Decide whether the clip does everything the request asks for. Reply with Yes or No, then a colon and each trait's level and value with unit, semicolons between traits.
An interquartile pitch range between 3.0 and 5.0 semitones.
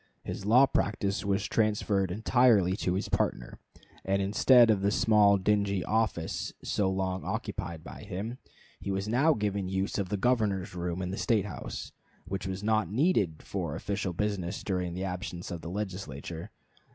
No: narrow, 2.5 semitones